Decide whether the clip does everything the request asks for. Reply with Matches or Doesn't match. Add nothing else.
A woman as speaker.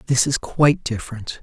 Doesn't match